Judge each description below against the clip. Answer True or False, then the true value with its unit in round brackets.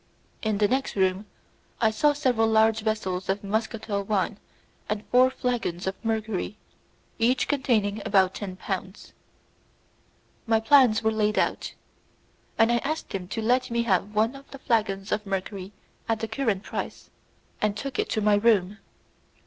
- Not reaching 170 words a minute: True (155 wpm)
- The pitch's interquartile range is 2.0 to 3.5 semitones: True (2.7 semitones)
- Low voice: False (215 Hz)